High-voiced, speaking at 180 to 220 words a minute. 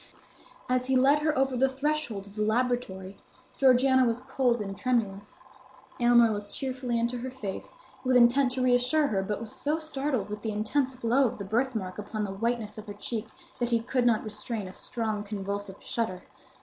Yes: high, 235 Hz; average, 190 wpm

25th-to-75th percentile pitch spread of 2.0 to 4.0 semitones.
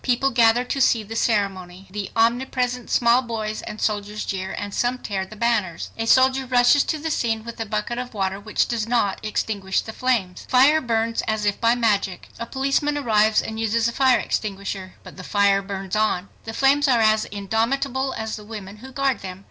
Yes: average, 3.4 semitones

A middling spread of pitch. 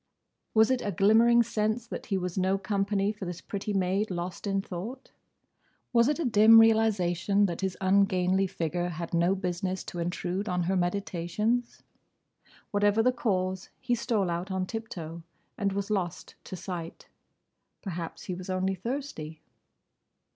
Yes: average, 3.2 semitones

